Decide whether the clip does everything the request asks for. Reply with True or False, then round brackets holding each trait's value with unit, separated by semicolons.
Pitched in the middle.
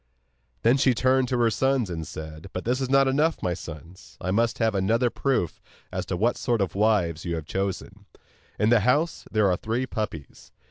False (110 Hz)